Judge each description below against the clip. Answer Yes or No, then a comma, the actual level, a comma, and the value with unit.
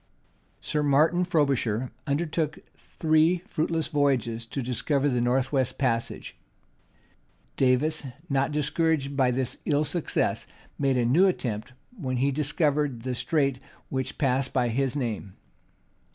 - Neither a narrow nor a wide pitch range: Yes, average, 3.2 semitones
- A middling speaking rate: No, slow, 125 wpm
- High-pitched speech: No, medium, 140 Hz